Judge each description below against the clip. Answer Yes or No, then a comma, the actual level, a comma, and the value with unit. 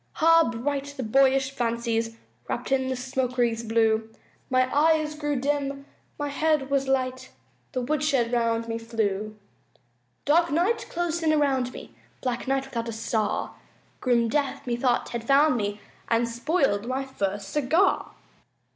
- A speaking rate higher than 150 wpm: No, average, 145 wpm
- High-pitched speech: Yes, very high, 260 Hz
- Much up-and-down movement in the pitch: No, average, 3.7 semitones